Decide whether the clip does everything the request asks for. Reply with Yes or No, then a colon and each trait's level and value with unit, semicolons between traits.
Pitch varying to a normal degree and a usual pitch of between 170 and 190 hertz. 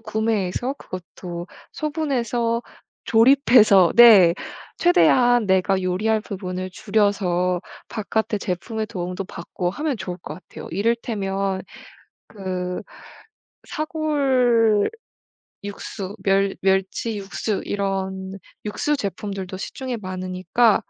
No: average, 3.7 semitones; high, 200 Hz